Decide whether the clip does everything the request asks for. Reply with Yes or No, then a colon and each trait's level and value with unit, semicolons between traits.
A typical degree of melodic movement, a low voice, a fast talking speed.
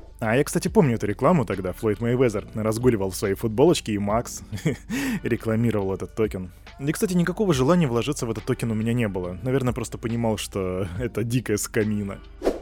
Yes: average, 4.0 semitones; low, 115 Hz; fast, 175 wpm